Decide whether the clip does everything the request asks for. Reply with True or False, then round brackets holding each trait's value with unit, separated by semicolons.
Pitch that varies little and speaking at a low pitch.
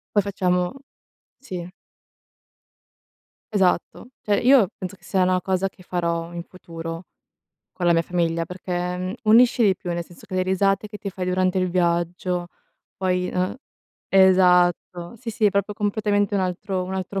False (1.9 semitones; 185 Hz)